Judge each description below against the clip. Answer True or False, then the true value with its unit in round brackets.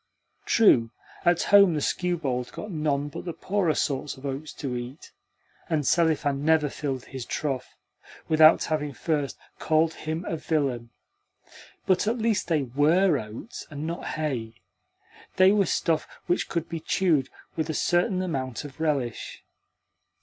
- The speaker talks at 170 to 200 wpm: False (150 wpm)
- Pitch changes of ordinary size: True (3.9 semitones)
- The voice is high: False (155 Hz)